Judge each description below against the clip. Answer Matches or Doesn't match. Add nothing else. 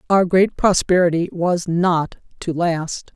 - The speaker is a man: Doesn't match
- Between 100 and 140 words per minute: Matches